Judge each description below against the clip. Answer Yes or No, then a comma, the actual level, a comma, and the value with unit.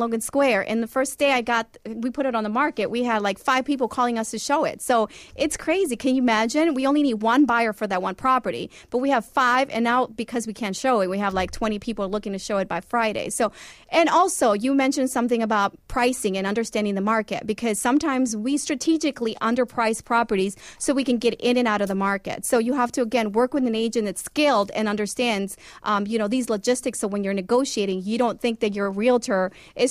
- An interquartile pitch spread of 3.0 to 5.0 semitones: Yes, average, 3.4 semitones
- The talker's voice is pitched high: Yes, high, 235 Hz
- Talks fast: Yes, fast, 235 wpm